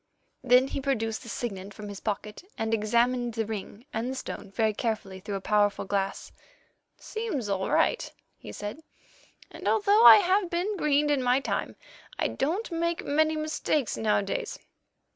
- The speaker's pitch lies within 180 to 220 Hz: No, high, 240 Hz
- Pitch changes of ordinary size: No, wide, 6.7 semitones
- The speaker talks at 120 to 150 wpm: No, average, 160 wpm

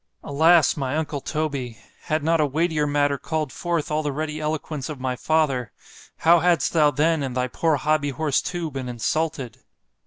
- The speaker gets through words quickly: No, average, 175 wpm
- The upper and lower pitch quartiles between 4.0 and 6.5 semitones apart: No, narrow, 2.6 semitones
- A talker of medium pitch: Yes, medium, 150 Hz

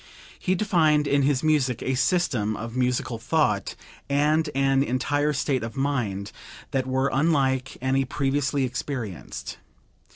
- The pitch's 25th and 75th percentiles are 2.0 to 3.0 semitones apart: Yes, narrow, 2.6 semitones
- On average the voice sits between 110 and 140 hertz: Yes, low, 135 Hz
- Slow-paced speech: Yes, slow, 130 wpm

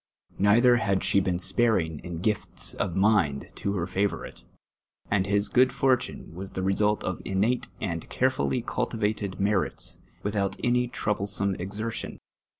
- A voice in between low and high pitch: No, low, 100 Hz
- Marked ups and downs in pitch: No, average, 2.7 semitones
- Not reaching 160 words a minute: Yes, average, 145 wpm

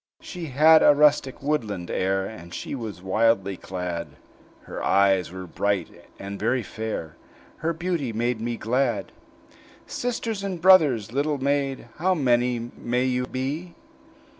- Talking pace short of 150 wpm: Yes, average, 140 wpm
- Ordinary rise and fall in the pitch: No, wide, 6.9 semitones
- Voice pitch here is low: Yes, low, 125 Hz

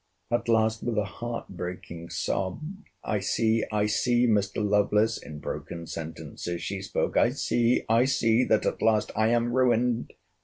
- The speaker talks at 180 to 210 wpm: No, average, 145 wpm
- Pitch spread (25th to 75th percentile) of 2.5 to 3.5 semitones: Yes, average, 3.2 semitones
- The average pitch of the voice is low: Yes, low, 110 Hz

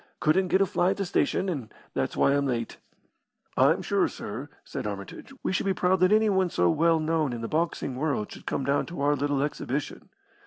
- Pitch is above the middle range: No, medium, 150 Hz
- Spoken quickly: Yes, fast, 210 wpm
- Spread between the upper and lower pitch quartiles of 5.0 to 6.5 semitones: Yes, average, 5.3 semitones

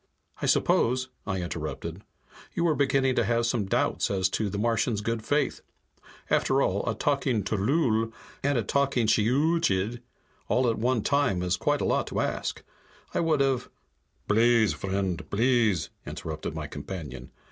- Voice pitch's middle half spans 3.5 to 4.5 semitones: No, average, 5.0 semitones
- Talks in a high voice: No, low, 115 Hz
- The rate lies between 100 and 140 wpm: No, average, 160 wpm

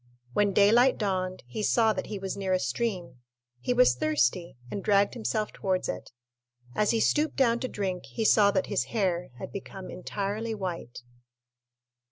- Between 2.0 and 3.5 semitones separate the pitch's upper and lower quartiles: Yes, average, 3.2 semitones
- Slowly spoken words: No, average, 170 wpm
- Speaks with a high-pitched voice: Yes, high, 200 Hz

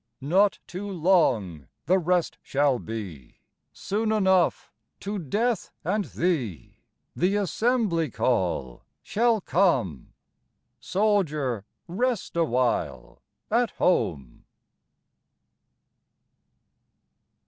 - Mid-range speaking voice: Yes, medium, 175 Hz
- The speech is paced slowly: Yes, slow, 80 wpm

